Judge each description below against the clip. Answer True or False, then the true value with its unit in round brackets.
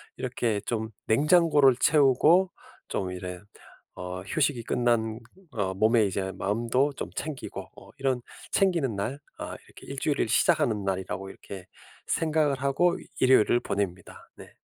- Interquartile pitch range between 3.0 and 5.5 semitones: False (6.1 semitones)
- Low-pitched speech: True (120 Hz)